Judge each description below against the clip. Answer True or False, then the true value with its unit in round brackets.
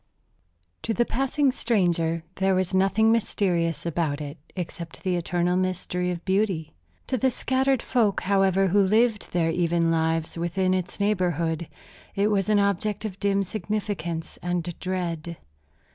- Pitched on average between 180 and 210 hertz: True (185 Hz)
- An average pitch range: True (3.3 semitones)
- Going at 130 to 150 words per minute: True (145 wpm)